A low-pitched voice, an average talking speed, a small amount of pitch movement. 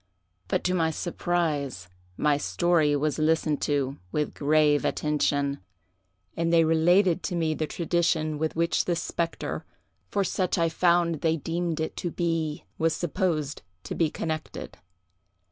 No: medium, 160 Hz; average, 145 wpm; narrow, 2.1 semitones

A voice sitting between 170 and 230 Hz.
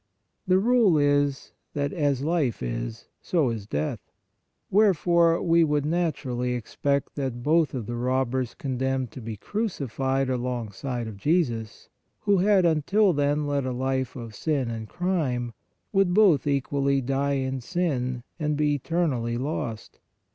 No: medium, 140 Hz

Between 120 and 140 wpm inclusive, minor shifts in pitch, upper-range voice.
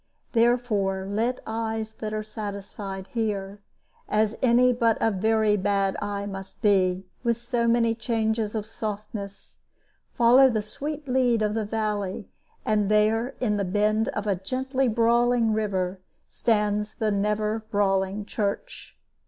Yes: slow, 135 wpm; narrow, 2.2 semitones; high, 215 Hz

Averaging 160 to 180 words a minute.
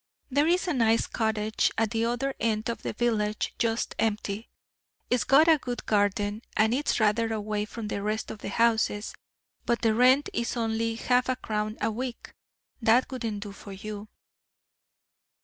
Yes: average, 170 wpm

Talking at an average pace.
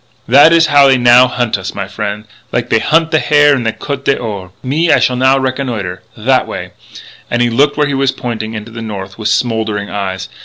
No: fast, 220 wpm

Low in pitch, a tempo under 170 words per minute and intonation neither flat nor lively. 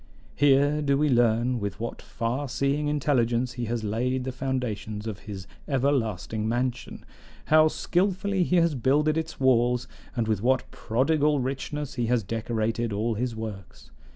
Yes: low, 125 Hz; average, 155 wpm; average, 4.0 semitones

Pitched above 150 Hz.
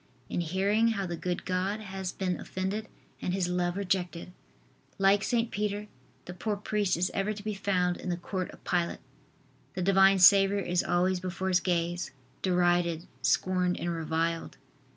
Yes: medium, 185 Hz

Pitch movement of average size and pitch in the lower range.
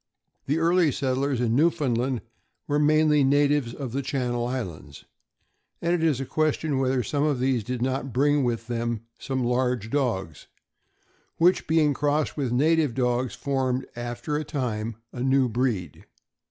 Yes: average, 3.4 semitones; low, 130 Hz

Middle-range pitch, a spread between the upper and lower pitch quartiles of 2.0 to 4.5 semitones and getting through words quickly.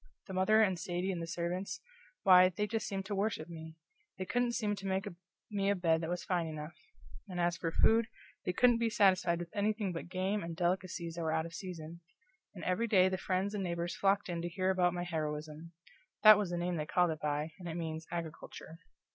Yes: medium, 180 Hz; narrow, 2.6 semitones; fast, 220 wpm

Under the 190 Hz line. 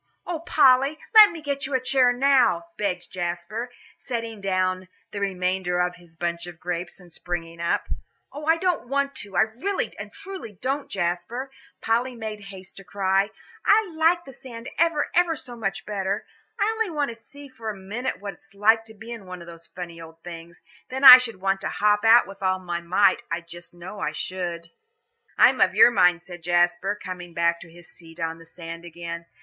No: high, 195 Hz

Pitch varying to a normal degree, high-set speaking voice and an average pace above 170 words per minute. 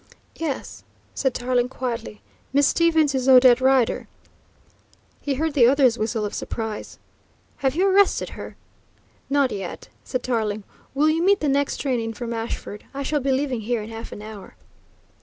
No: average, 3.9 semitones; very high, 255 Hz; average, 165 wpm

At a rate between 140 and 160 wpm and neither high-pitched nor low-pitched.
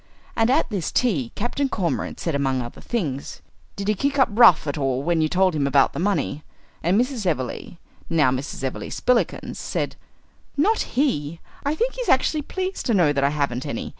No: average, 195 wpm; medium, 175 Hz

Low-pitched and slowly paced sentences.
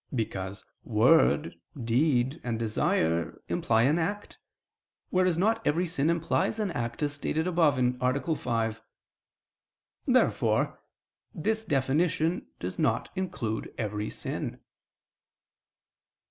No: medium, 145 Hz; slow, 105 wpm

